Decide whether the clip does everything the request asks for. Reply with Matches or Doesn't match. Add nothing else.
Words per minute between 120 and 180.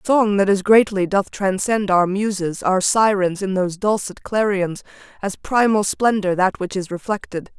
Matches